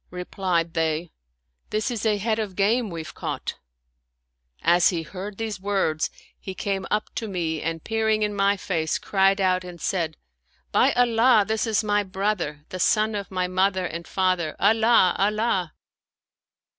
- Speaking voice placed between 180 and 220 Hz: Yes, high, 190 Hz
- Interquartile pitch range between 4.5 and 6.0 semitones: No, average, 3.6 semitones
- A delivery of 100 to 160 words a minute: No, average, 170 wpm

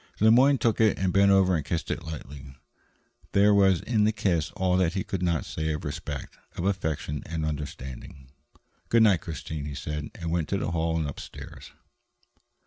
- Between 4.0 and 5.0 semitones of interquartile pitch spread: Yes, average, 4.6 semitones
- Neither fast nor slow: Yes, average, 190 wpm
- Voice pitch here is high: No, very low, 85 Hz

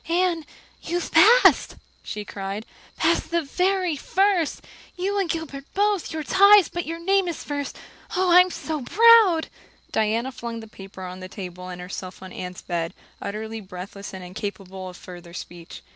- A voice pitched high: Yes, very high, 255 Hz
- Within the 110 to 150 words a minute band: No, average, 160 wpm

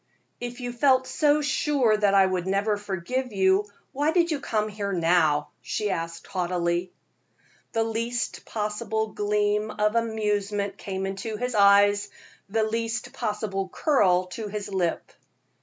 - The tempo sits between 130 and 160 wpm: Yes, average, 140 wpm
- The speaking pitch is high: Yes, high, 210 Hz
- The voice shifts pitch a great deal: No, average, 3.1 semitones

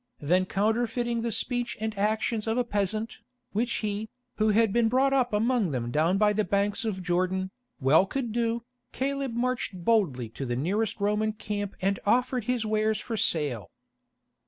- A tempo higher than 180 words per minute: No, average, 170 wpm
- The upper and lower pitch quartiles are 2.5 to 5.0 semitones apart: Yes, average, 3.6 semitones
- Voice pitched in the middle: No, high, 215 Hz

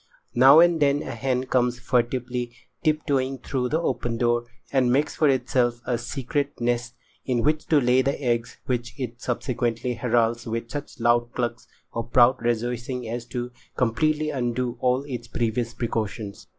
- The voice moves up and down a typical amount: No, narrow, 1.9 semitones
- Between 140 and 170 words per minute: Yes, average, 165 wpm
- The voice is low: Yes, low, 125 Hz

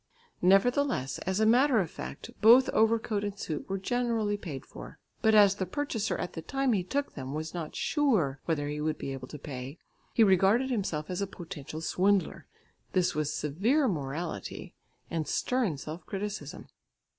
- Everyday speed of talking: Yes, average, 170 wpm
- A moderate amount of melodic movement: No, wide, 6.5 semitones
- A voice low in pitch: No, high, 190 Hz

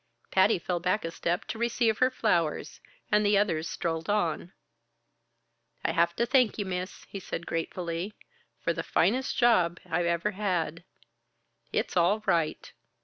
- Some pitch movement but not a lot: Yes, average, 3.9 semitones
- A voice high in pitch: No, medium, 180 Hz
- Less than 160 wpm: Yes, average, 150 wpm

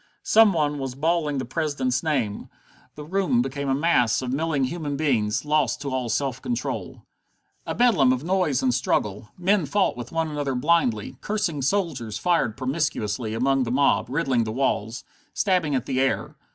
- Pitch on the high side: No, medium, 140 Hz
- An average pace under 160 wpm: No, average, 170 wpm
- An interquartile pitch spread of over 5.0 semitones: No, average, 4.5 semitones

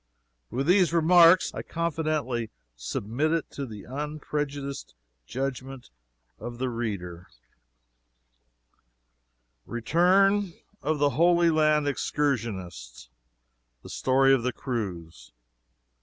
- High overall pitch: No, low, 135 Hz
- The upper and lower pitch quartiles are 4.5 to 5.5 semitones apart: Yes, average, 5.2 semitones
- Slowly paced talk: Yes, slow, 95 wpm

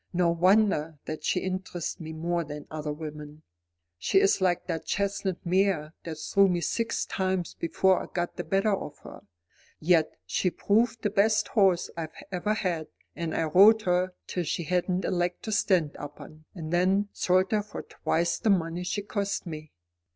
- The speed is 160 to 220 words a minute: Yes, average, 180 wpm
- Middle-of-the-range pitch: Yes, medium, 180 Hz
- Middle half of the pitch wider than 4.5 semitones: No, average, 3.3 semitones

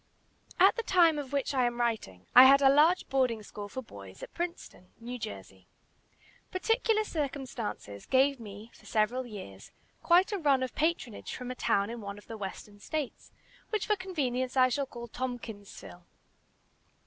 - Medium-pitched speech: No, very high, 255 Hz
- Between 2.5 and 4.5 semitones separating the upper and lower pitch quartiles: No, wide, 5.6 semitones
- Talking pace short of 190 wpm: Yes, average, 170 wpm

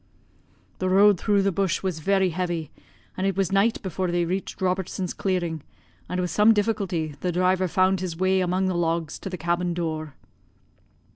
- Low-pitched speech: No, medium, 185 Hz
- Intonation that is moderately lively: No, narrow, 1.9 semitones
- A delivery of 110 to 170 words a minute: No, average, 180 wpm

